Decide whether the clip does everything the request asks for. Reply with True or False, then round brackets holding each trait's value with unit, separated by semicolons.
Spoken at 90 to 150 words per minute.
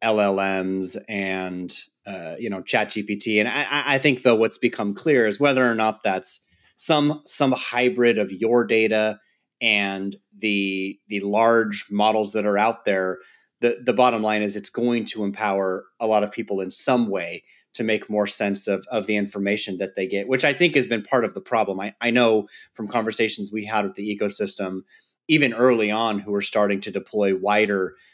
False (190 wpm)